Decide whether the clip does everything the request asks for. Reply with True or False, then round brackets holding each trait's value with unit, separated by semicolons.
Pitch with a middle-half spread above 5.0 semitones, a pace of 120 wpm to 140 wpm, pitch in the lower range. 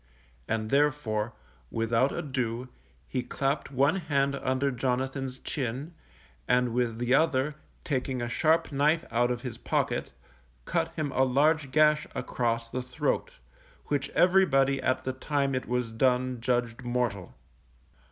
False (2.5 semitones; 135 wpm; 130 Hz)